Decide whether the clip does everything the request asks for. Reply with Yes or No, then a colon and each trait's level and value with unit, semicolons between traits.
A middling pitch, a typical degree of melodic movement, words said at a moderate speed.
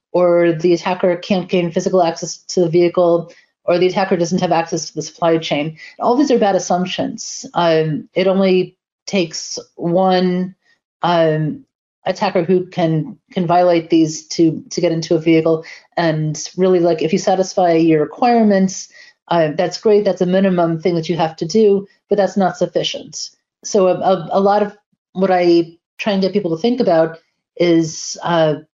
No: medium, 180 Hz; narrow, 2.3 semitones; average, 175 wpm